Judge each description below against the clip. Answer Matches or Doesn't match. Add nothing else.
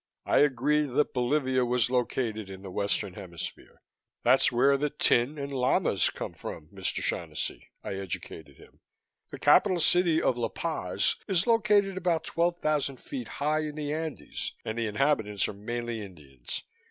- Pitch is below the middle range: Matches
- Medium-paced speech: Matches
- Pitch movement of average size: Doesn't match